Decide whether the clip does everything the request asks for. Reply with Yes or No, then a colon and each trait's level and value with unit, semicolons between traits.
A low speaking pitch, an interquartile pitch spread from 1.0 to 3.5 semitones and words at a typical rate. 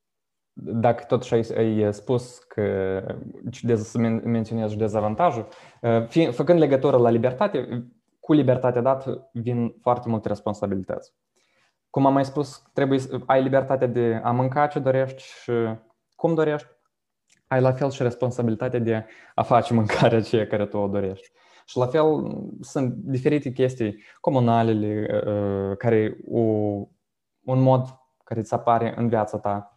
Yes: low, 120 Hz; average, 3.0 semitones; average, 140 wpm